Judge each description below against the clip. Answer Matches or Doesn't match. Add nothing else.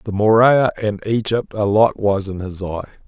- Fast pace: Doesn't match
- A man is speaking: Matches